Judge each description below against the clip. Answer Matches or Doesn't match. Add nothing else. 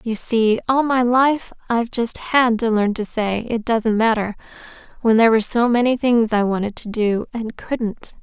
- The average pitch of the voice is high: Matches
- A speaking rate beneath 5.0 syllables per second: Matches